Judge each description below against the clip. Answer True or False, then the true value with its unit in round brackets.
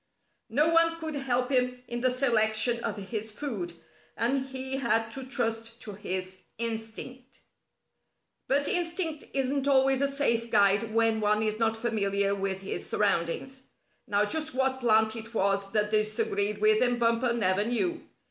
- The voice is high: True (230 Hz)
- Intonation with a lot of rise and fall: False (3.8 semitones)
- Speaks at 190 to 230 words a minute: False (155 wpm)